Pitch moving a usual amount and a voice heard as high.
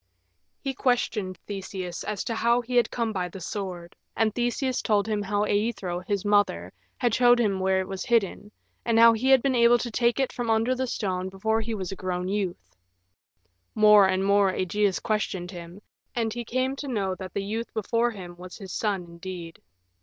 Yes: average, 3.8 semitones; high, 205 Hz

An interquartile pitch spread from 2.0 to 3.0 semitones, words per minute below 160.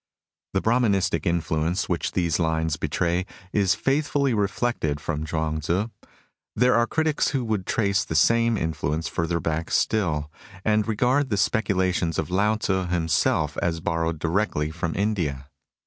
No: average, 5.0 semitones; average, 150 wpm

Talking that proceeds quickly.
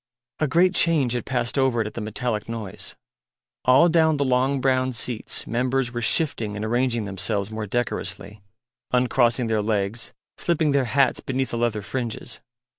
No: average, 165 wpm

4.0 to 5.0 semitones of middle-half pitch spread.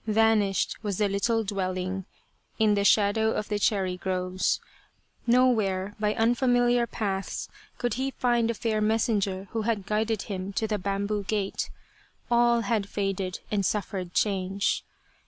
No: narrow, 2.5 semitones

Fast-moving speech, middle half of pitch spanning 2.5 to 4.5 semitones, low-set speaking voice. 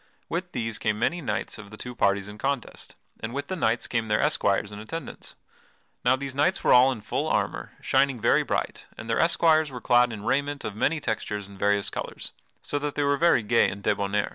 No: fast, 220 wpm; wide, 5.4 semitones; low, 120 Hz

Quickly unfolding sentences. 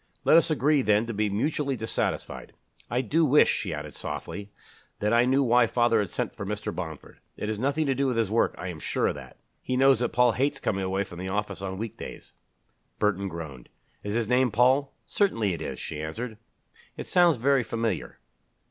Yes: fast, 210 wpm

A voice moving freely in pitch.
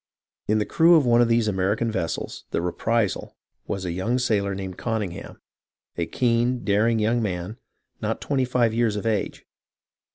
No: average, 3.4 semitones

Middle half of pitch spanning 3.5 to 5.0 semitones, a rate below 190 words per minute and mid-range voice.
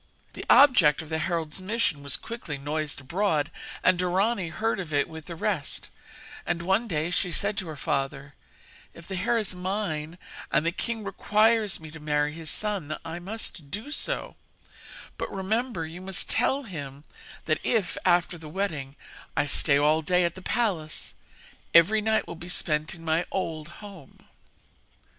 Yes: average, 4.7 semitones; average, 170 wpm; medium, 175 Hz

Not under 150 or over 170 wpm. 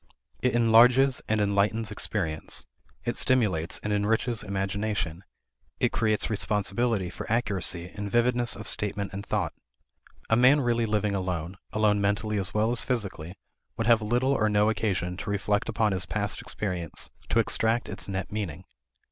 Yes: average, 155 wpm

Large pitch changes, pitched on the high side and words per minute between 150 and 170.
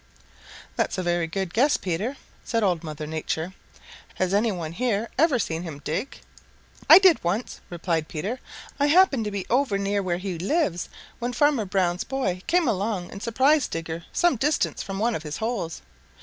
No: wide, 6.2 semitones; high, 200 Hz; average, 180 wpm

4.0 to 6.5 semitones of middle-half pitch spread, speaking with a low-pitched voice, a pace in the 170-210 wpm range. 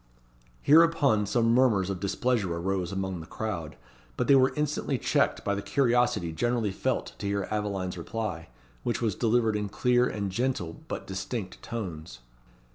No: average, 4.5 semitones; low, 105 Hz; average, 155 wpm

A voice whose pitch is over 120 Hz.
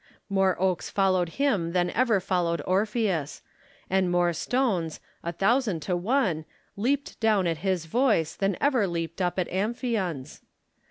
Yes: high, 190 Hz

